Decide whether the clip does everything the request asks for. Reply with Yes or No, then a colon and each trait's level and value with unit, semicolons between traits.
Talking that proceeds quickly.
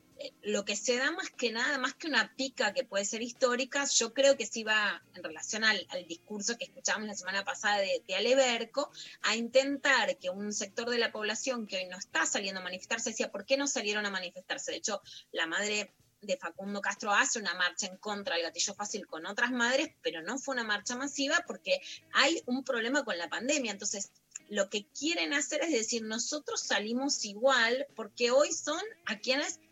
Yes: fast, 205 wpm